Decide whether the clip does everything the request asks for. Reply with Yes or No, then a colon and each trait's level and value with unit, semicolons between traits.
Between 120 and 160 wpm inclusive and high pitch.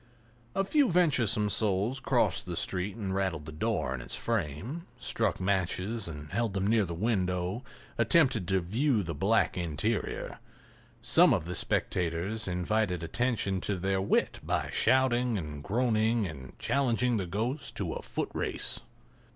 No: average, 150 wpm; low, 100 Hz